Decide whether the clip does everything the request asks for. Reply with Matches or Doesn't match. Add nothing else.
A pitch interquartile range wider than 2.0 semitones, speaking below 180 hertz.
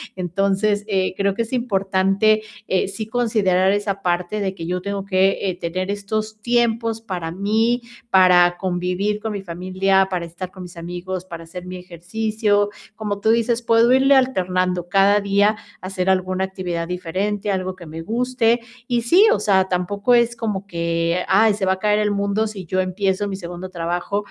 Doesn't match